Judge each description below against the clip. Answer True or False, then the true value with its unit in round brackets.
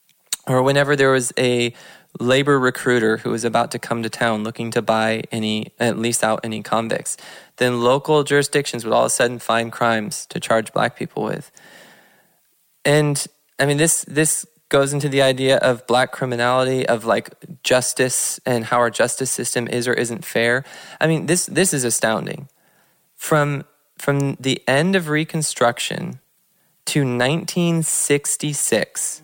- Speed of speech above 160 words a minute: False (155 wpm)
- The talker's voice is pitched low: True (130 Hz)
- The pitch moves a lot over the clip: False (3.9 semitones)